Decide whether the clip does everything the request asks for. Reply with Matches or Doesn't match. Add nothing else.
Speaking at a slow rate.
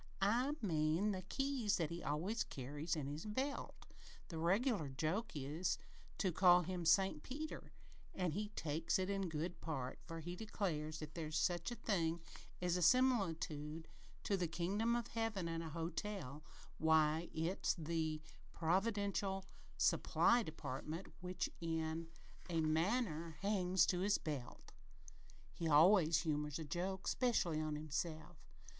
Doesn't match